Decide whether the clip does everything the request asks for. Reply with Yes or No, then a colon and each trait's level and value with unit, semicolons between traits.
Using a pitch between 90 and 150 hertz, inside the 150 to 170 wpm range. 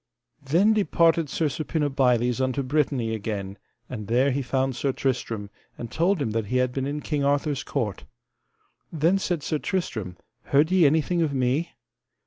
Yes: medium, 140 Hz; average, 160 wpm